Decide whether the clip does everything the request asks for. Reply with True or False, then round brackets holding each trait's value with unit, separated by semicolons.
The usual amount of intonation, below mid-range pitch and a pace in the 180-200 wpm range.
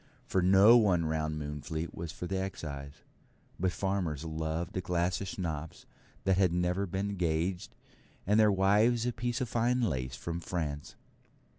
False (3.8 semitones; 90 Hz; 160 wpm)